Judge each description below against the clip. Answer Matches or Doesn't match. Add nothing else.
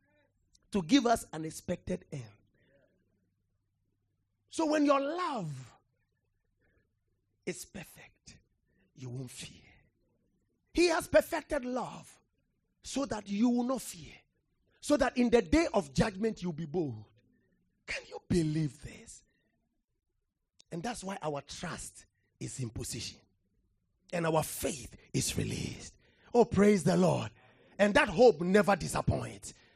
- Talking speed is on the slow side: Matches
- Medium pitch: Matches